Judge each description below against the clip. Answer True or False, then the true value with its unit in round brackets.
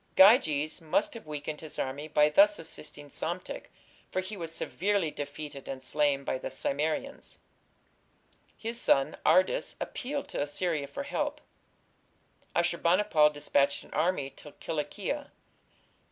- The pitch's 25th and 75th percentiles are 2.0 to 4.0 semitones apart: False (5.5 semitones)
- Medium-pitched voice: True (155 Hz)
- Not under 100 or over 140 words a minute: True (135 wpm)